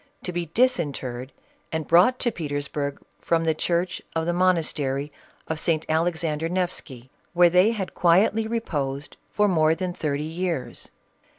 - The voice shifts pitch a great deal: No, average, 3.4 semitones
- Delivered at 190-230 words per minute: No, average, 140 wpm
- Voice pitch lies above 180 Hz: No, medium, 165 Hz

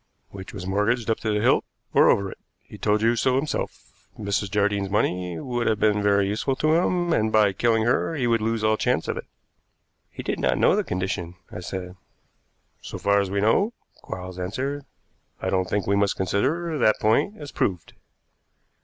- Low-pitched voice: Yes, low, 105 Hz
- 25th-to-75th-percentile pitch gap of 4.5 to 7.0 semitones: No, average, 3.6 semitones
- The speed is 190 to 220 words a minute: Yes, average, 195 wpm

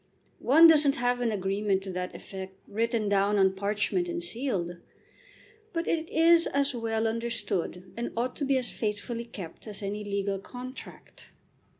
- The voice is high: Yes, high, 225 Hz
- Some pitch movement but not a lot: Yes, average, 4.6 semitones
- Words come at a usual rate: Yes, average, 160 wpm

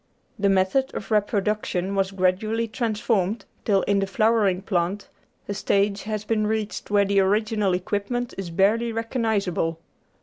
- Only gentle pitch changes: Yes, narrow, 2.2 semitones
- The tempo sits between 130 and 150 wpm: Yes, average, 140 wpm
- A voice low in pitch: No, high, 205 Hz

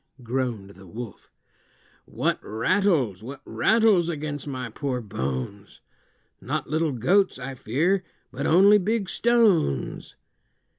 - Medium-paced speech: No, slow, 110 wpm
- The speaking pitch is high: No, medium, 140 Hz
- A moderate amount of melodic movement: No, wide, 8.8 semitones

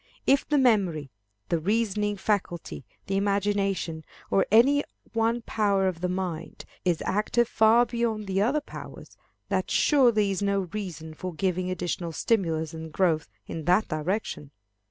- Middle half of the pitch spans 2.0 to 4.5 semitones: Yes, average, 4.1 semitones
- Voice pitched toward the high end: Yes, high, 195 Hz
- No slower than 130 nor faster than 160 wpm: Yes, average, 145 wpm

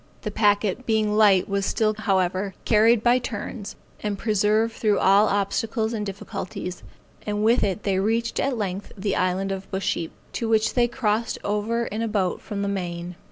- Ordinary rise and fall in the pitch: No, narrow, 2.3 semitones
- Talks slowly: No, average, 175 wpm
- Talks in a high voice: Yes, high, 210 Hz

